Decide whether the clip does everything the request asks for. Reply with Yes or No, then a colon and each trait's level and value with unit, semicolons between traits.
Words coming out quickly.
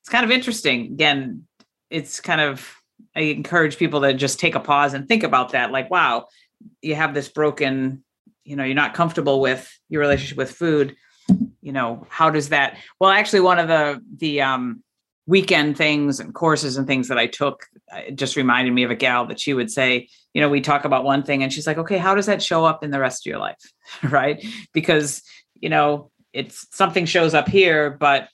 Yes: fast, 210 wpm